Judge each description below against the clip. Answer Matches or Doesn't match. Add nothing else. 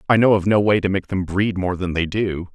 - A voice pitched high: Doesn't match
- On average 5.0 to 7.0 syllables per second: Matches